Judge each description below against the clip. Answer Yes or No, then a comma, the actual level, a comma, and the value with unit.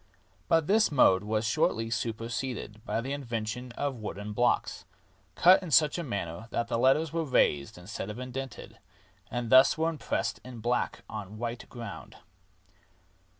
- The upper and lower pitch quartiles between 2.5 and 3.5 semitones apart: No, average, 3.9 semitones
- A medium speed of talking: Yes, average, 160 wpm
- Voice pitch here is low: Yes, low, 120 Hz